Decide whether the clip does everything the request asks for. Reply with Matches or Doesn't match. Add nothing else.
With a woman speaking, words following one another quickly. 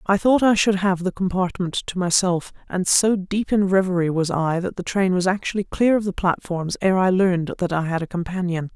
Matches